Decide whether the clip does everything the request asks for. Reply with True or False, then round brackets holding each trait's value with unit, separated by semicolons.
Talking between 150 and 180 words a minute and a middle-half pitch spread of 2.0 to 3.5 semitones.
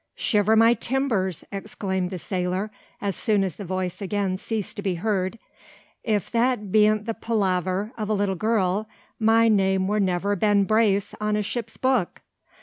True (165 wpm; 2.5 semitones)